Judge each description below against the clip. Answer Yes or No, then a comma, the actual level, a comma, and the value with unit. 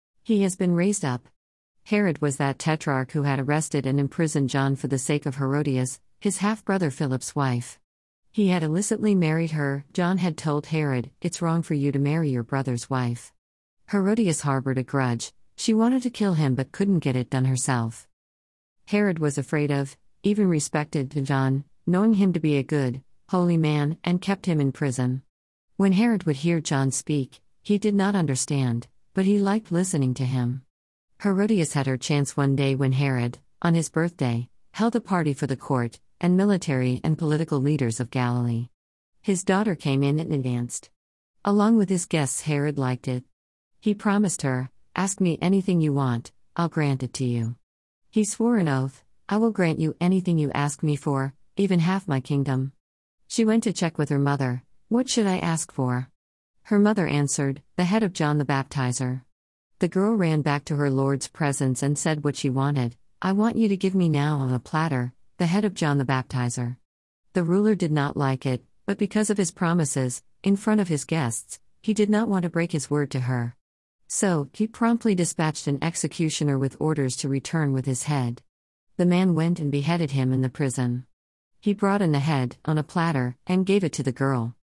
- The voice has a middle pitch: Yes, medium, 145 Hz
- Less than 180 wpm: No, average, 195 wpm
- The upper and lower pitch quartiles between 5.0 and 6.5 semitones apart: Yes, wide, 5.5 semitones